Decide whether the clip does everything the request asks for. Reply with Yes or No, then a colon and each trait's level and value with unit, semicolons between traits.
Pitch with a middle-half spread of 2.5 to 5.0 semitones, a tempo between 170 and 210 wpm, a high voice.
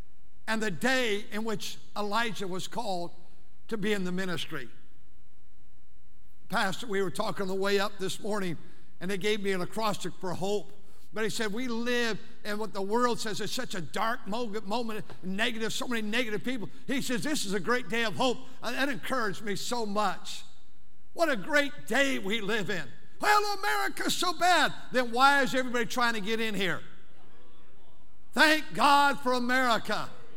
Yes: average, 4.1 semitones; average, 175 wpm; high, 220 Hz